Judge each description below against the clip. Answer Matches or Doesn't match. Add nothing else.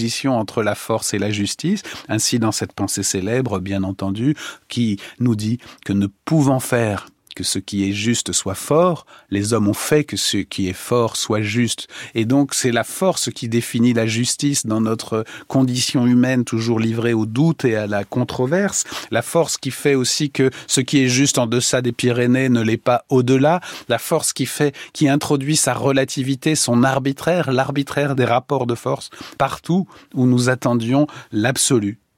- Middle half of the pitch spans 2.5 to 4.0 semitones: Matches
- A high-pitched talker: Doesn't match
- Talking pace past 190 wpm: Doesn't match